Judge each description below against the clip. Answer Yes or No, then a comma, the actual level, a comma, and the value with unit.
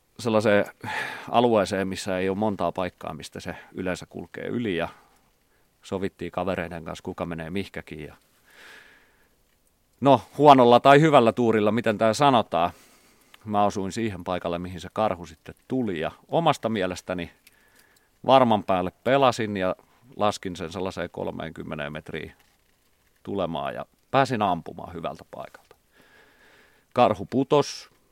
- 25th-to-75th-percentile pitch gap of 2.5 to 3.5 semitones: No, average, 4.0 semitones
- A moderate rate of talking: Yes, average, 120 wpm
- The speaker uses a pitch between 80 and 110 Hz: Yes, very low, 95 Hz